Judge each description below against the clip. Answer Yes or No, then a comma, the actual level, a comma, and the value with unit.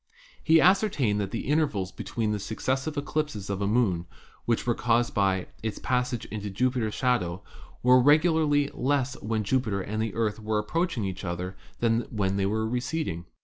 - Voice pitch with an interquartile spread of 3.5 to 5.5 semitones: Yes, average, 4.6 semitones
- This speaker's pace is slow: No, average, 165 wpm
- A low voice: Yes, low, 115 Hz